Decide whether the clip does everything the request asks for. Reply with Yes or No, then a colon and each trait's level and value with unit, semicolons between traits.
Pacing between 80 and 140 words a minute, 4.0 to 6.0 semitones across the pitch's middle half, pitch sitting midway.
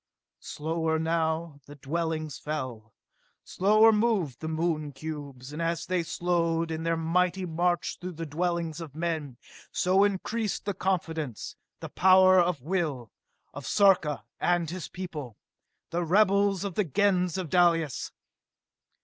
No: slow, 135 wpm; average, 2.9 semitones; medium, 165 Hz